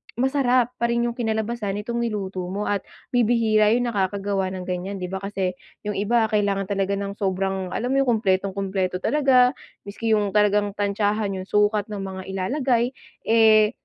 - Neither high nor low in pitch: No, high, 205 Hz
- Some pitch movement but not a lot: Yes, average, 3.0 semitones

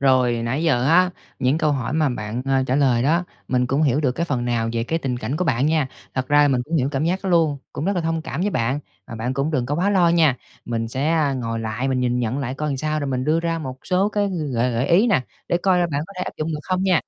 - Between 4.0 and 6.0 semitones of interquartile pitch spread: Yes, average, 4.6 semitones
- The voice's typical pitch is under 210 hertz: Yes, medium, 140 Hz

